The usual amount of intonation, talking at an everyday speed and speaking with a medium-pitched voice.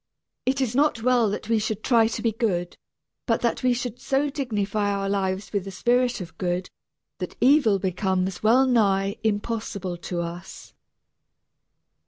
No: average, 4.1 semitones; average, 160 wpm; high, 215 Hz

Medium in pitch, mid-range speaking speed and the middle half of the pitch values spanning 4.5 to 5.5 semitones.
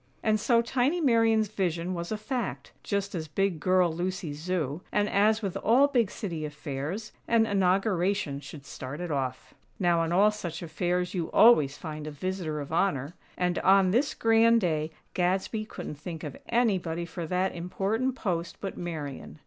Yes: medium, 180 Hz; average, 170 wpm; average, 4.8 semitones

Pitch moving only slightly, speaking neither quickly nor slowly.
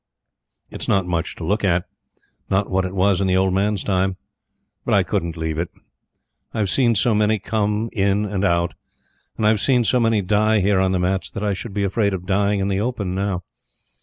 No: narrow, 2.2 semitones; fast, 210 wpm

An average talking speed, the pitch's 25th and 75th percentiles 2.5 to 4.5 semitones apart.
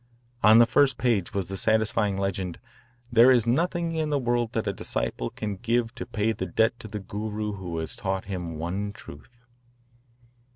Yes: average, 180 wpm; average, 3.6 semitones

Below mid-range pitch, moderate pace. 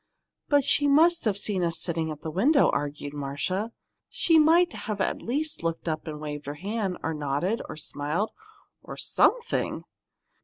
No: medium, 185 Hz; average, 165 wpm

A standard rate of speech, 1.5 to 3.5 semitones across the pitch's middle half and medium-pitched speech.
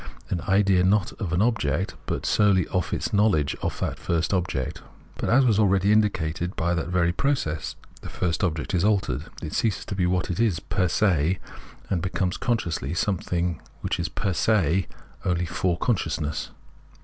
No: average, 170 wpm; average, 3.2 semitones; very low, 90 Hz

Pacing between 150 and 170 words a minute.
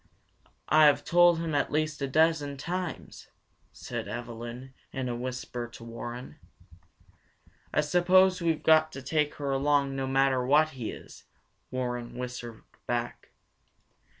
No: average, 140 wpm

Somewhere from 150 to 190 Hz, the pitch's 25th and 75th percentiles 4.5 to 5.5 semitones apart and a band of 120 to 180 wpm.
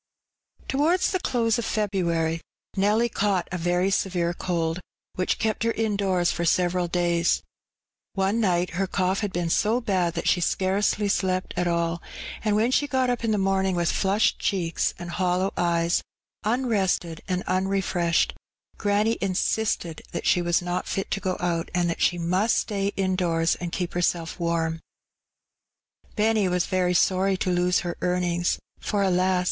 No: medium, 185 Hz; average, 2.7 semitones; average, 170 wpm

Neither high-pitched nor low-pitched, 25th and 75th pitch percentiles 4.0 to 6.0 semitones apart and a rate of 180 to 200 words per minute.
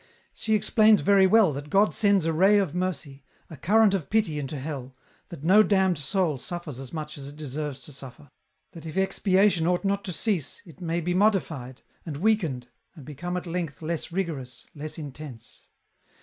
Yes: medium, 165 Hz; average, 5.1 semitones; average, 185 wpm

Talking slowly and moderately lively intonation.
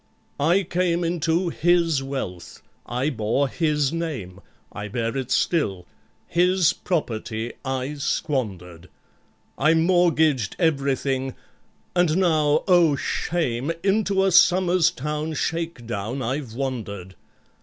No: slow, 100 wpm; wide, 5.7 semitones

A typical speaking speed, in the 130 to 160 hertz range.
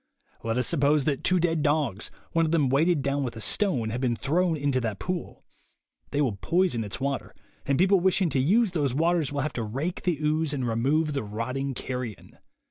No: fast, 210 wpm; medium, 140 Hz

